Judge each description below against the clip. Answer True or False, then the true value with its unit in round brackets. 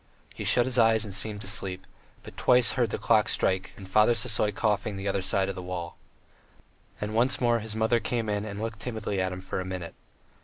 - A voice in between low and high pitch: False (105 Hz)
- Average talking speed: False (225 wpm)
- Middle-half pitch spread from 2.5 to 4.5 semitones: True (2.9 semitones)